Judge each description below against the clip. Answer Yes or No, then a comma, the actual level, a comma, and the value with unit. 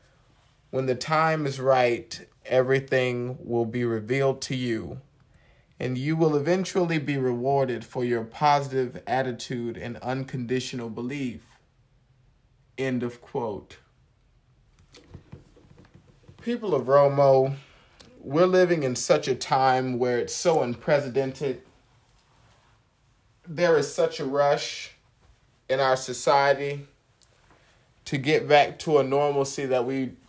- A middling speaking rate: No, slow, 110 wpm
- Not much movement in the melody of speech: Yes, narrow, 2.3 semitones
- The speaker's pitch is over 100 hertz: Yes, low, 130 Hz